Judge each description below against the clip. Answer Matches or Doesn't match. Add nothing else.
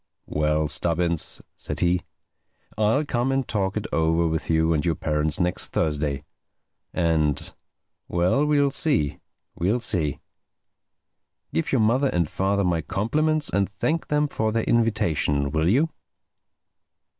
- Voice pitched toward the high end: Doesn't match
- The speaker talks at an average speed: Doesn't match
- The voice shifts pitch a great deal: Matches